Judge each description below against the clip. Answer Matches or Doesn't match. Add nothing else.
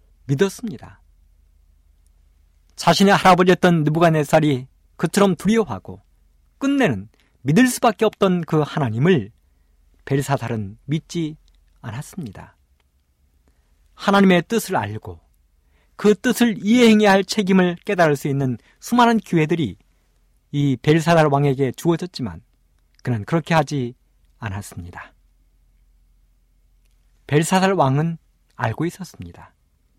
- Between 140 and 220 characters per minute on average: Doesn't match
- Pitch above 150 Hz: Doesn't match